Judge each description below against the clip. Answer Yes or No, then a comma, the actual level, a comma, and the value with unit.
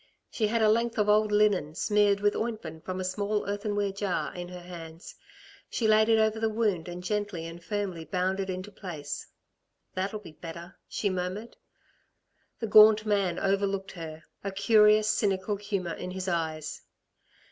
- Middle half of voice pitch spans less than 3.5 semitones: Yes, average, 2.9 semitones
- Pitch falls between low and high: No, high, 195 Hz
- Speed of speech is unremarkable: Yes, average, 170 wpm